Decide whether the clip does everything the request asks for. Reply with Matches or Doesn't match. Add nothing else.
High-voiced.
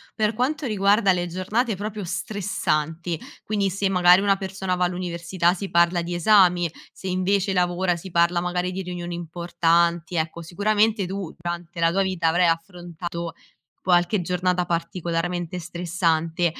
Doesn't match